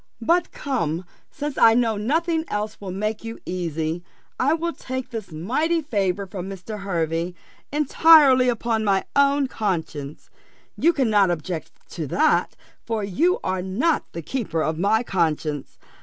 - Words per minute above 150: No, average, 145 wpm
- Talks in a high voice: Yes, high, 210 Hz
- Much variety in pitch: Yes, wide, 7.3 semitones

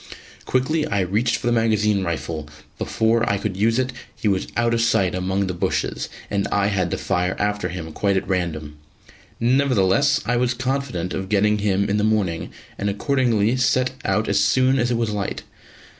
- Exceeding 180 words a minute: Yes, average, 190 wpm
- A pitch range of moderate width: Yes, average, 4.0 semitones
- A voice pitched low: Yes, low, 105 Hz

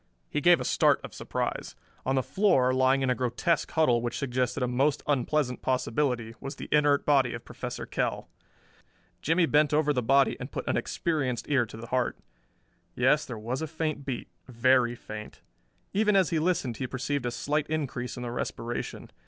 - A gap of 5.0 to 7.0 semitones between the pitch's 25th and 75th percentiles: No, average, 3.4 semitones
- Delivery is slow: No, average, 185 wpm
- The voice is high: No, low, 130 Hz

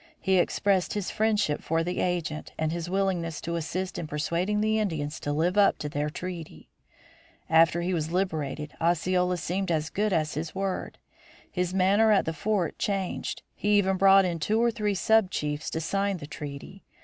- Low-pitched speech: No, medium, 180 Hz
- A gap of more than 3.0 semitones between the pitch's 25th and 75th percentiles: Yes, average, 3.5 semitones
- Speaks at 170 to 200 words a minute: Yes, average, 185 wpm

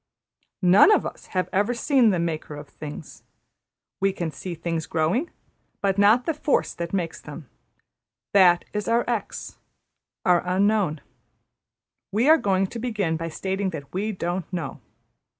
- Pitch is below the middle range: No, high, 190 Hz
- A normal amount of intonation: Yes, average, 4.2 semitones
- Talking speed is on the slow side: No, average, 155 wpm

